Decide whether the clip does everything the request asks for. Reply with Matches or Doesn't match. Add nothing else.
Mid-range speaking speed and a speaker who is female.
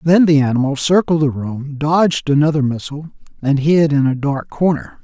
Doesn't match